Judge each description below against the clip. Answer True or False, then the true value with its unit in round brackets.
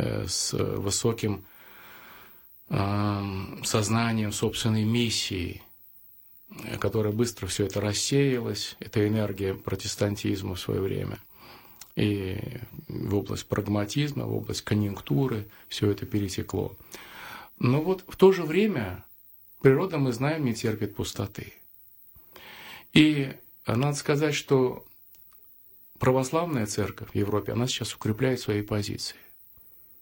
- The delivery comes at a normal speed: False (100 wpm)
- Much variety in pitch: False (3.5 semitones)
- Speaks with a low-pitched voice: True (110 Hz)